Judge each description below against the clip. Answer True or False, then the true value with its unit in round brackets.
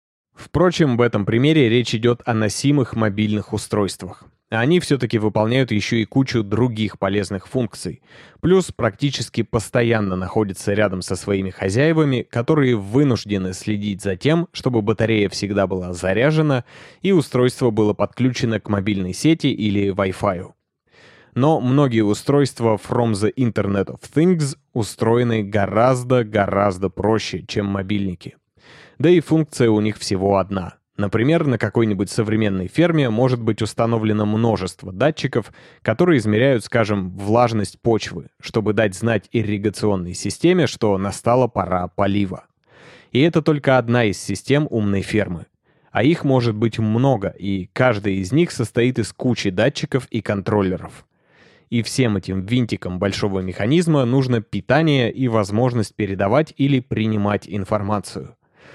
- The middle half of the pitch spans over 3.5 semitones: True (4.2 semitones)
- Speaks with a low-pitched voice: True (110 Hz)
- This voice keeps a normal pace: True (130 wpm)